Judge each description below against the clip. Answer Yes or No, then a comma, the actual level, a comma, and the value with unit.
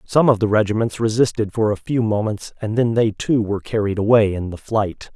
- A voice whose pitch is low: Yes, low, 110 Hz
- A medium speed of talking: No, fast, 220 wpm